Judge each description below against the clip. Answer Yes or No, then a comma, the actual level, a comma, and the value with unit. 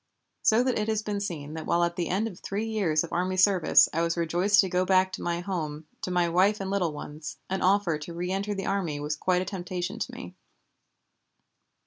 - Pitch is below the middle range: No, medium, 180 Hz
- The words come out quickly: Yes, fast, 220 wpm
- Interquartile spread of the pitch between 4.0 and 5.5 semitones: No, average, 2.8 semitones